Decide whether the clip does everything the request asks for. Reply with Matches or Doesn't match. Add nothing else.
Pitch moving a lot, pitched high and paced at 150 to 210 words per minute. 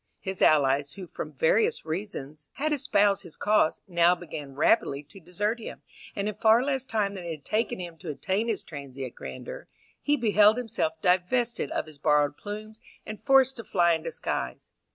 Matches